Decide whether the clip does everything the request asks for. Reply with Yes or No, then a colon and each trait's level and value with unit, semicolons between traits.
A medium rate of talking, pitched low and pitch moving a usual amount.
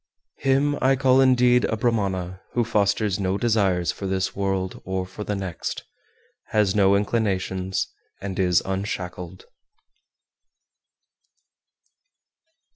No: slow, 115 wpm; low, 100 Hz; average, 3.4 semitones